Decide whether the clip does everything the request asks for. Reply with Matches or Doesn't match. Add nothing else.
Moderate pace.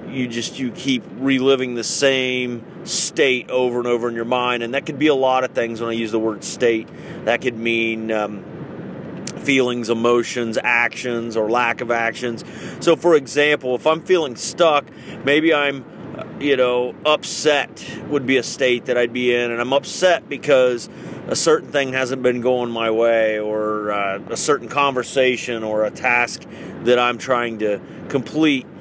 Matches